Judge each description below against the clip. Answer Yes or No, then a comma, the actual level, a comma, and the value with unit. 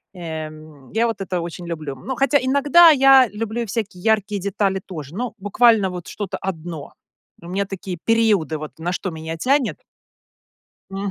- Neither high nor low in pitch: No, high, 195 Hz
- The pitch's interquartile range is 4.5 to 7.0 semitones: Yes, average, 5.3 semitones